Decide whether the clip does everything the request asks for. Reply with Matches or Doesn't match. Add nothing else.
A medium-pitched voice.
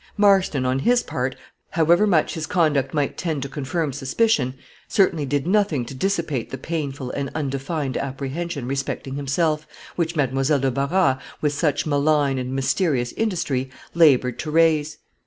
Matches